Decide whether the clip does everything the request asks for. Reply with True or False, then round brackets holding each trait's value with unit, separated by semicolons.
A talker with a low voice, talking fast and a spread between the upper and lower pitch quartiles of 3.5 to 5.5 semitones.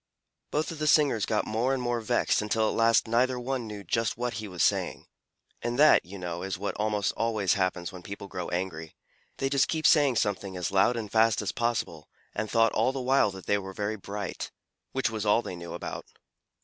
True (110 Hz; 220 wpm; 3.9 semitones)